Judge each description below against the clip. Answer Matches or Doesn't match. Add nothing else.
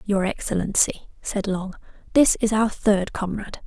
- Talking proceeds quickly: Doesn't match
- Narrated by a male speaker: Doesn't match